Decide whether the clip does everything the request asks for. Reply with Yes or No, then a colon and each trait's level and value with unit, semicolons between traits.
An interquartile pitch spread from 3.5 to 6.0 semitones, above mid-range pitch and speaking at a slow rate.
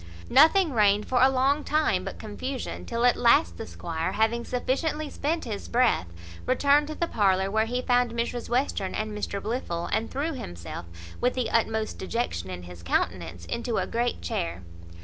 No: wide, 5.4 semitones; high, 230 Hz; average, 175 wpm